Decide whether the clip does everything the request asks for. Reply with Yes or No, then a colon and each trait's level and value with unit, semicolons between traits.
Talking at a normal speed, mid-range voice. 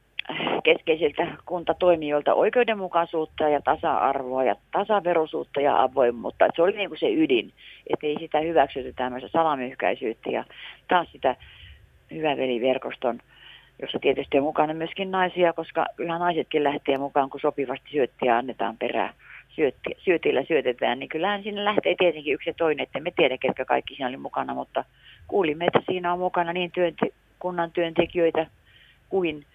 Yes: average, 140 wpm; medium, 165 Hz